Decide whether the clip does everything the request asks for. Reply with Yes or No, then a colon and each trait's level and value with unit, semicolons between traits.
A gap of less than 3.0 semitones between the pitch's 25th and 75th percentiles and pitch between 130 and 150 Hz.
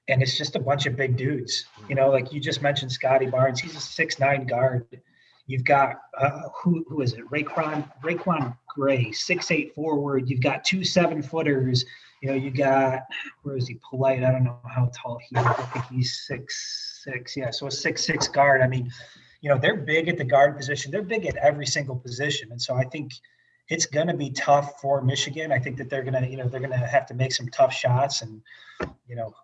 Yes: narrow, 2.6 semitones; low, 135 Hz